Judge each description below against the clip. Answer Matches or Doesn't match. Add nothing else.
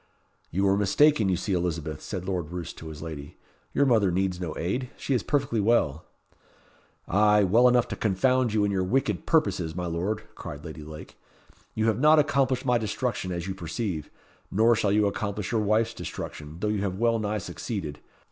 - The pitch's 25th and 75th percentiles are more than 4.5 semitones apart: Matches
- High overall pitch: Doesn't match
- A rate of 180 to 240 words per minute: Matches